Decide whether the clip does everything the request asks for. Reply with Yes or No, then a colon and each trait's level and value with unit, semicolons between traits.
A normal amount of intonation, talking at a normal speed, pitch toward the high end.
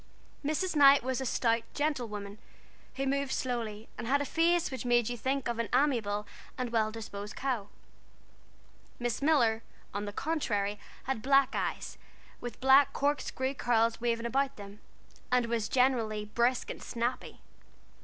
Yes: average, 3.5 semitones; average, 155 wpm; high, 245 Hz